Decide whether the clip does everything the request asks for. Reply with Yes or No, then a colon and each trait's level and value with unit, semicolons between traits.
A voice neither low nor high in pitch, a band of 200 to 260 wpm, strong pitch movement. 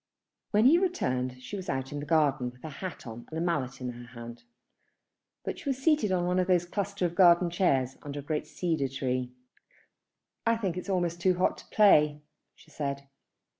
Yes: medium, 160 Hz; fast, 205 wpm; wide, 5.8 semitones